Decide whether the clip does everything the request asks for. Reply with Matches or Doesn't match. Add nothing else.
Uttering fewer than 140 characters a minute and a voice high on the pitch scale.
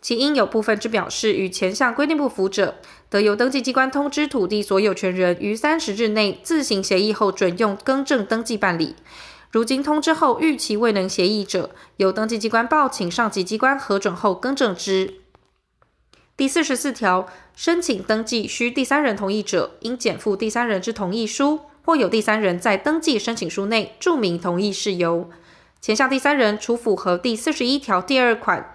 Doesn't match